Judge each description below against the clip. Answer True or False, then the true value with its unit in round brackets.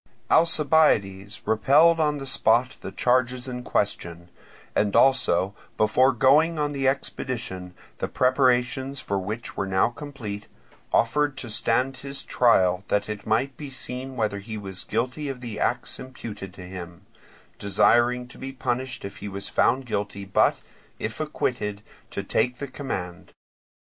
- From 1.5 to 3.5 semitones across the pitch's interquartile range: False (4.8 semitones)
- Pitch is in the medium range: False (120 Hz)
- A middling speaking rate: True (145 wpm)